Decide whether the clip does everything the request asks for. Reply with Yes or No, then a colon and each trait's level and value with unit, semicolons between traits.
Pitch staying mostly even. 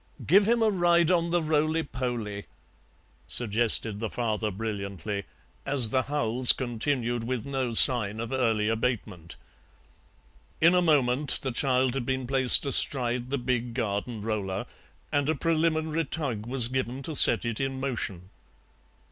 No: average, 4.2 semitones